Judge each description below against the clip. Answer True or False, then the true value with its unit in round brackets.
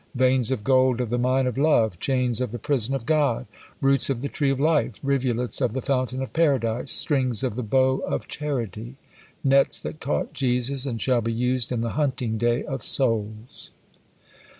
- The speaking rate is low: False (190 wpm)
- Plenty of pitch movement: False (2.5 semitones)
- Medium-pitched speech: False (130 Hz)